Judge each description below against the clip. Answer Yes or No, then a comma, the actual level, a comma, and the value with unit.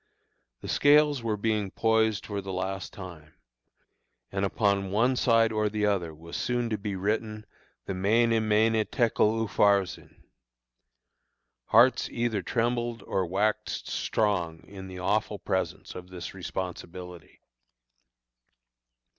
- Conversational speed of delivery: No, slow, 125 wpm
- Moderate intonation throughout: Yes, average, 3.1 semitones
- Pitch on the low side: Yes, low, 105 Hz